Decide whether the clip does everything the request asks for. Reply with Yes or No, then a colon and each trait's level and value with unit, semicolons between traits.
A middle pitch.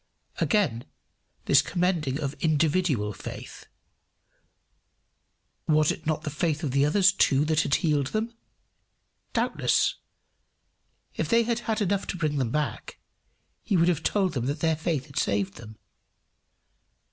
Yes: medium, 155 Hz